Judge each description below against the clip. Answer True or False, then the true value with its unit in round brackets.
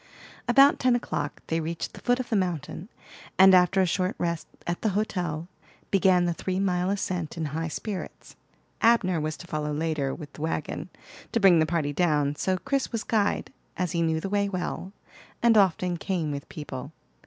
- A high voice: False (180 Hz)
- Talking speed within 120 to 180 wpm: False (190 wpm)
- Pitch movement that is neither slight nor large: True (3.6 semitones)